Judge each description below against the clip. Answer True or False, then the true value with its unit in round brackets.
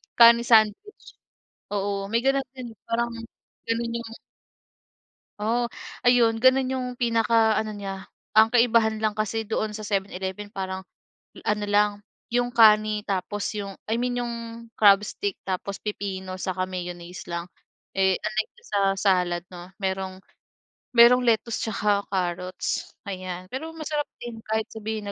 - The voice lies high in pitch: True (215 Hz)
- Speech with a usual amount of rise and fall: True (3.3 semitones)